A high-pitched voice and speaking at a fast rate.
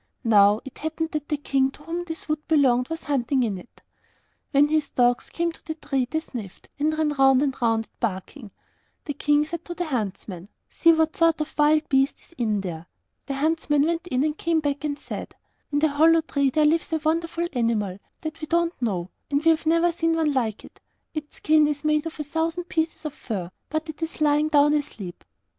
Yes: very high, 295 Hz; fast, 220 wpm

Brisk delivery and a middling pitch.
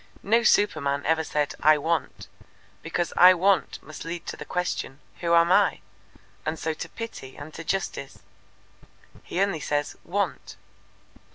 No: average, 150 wpm; medium, 165 Hz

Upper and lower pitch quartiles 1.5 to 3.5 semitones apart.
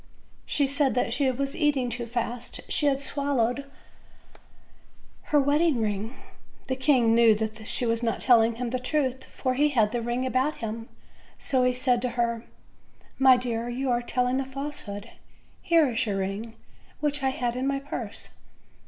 Yes: average, 2.8 semitones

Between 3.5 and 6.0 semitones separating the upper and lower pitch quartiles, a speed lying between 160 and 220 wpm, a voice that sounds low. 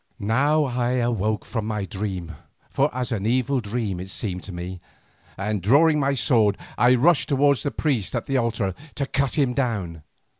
Yes: average, 5.2 semitones; average, 180 wpm; low, 115 Hz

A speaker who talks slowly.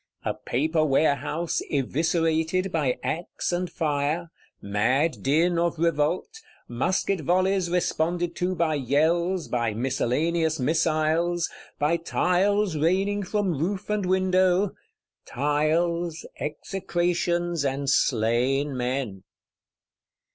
Yes: slow, 95 wpm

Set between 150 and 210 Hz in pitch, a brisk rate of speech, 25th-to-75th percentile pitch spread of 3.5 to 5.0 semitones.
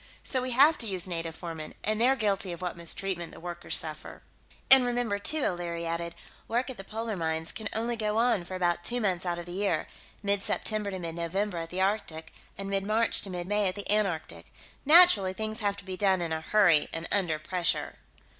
Yes: high, 190 Hz; fast, 220 wpm; average, 3.9 semitones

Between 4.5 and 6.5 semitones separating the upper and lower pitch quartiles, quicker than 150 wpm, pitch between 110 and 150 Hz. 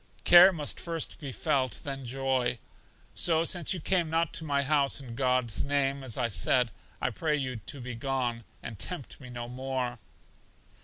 No: average, 3.4 semitones; average, 175 wpm; low, 135 Hz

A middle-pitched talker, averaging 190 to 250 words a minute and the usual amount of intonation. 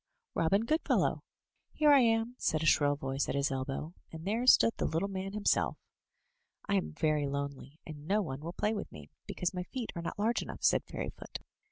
No: medium, 170 Hz; average, 200 wpm; wide, 6.6 semitones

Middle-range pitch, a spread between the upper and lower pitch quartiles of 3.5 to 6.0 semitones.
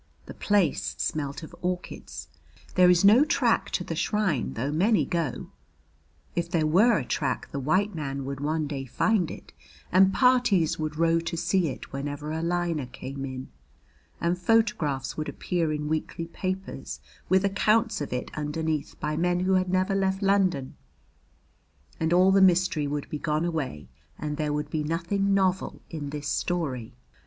Yes: medium, 165 Hz; average, 4.0 semitones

